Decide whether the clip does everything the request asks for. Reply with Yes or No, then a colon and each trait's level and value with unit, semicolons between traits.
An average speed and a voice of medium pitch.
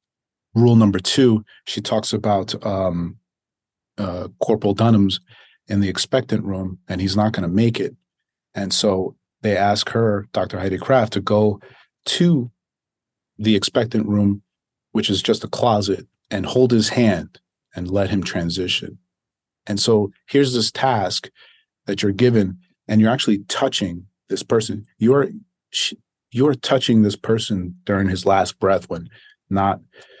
No: average, 145 wpm; low, 105 Hz